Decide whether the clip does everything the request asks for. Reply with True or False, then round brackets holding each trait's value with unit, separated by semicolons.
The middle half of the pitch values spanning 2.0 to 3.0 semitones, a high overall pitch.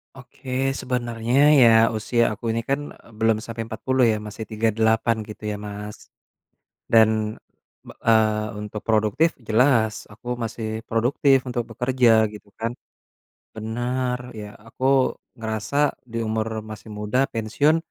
False (2.4 semitones; 115 Hz)